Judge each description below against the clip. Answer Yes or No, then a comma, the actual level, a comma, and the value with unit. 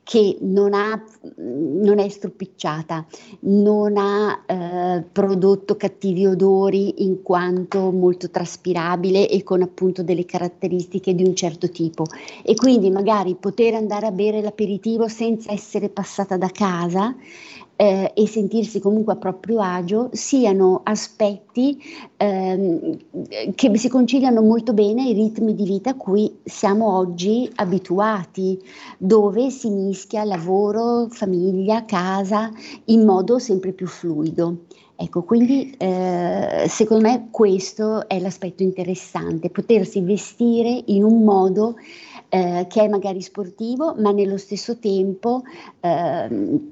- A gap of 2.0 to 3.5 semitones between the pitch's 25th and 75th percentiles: Yes, average, 2.8 semitones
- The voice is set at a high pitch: Yes, high, 200 Hz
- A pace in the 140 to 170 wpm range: No, average, 120 wpm